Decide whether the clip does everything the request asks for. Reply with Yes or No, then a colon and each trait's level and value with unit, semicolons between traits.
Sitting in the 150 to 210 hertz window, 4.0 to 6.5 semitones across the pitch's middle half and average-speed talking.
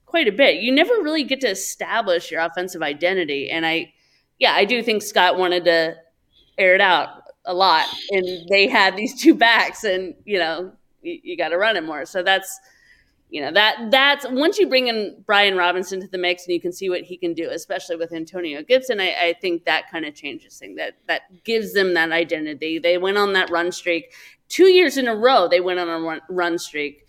No: medium, 185 Hz; wide, 5.4 semitones; fast, 225 wpm